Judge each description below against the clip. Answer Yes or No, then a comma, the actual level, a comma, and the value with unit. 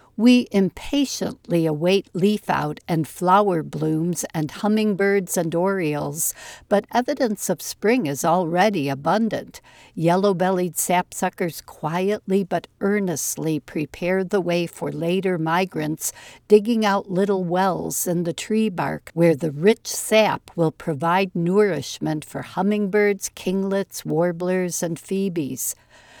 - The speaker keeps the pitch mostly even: No, average, 3.3 semitones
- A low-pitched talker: No, medium, 185 Hz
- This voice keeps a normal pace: No, slow, 120 wpm